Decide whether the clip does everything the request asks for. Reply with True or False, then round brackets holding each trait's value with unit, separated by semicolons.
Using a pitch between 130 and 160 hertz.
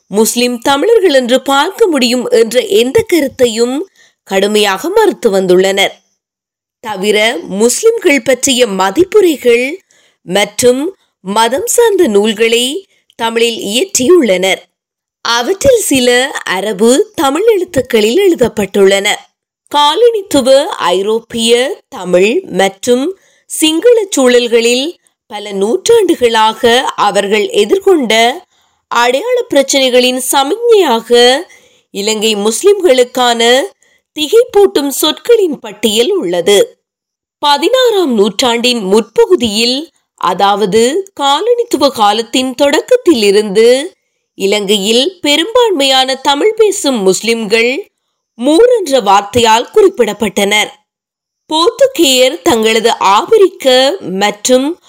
False (260 Hz)